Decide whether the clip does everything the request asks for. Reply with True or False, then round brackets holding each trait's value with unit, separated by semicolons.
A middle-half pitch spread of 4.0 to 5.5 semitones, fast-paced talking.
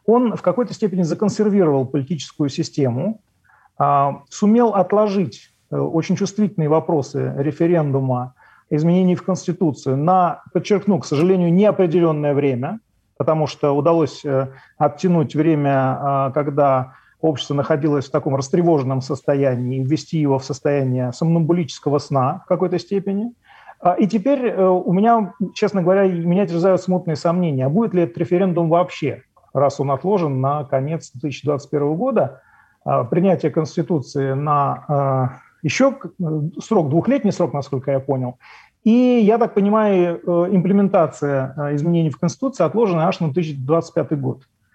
False (4.7 semitones; 120 wpm)